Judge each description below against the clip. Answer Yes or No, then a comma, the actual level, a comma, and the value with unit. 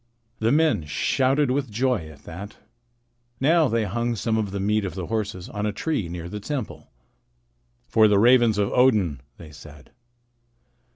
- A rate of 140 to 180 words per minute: Yes, average, 165 wpm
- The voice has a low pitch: Yes, low, 105 Hz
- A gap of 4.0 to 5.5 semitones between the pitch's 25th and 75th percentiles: Yes, average, 5.0 semitones